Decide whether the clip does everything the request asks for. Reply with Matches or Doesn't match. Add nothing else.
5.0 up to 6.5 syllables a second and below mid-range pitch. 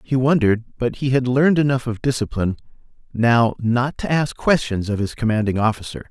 Matches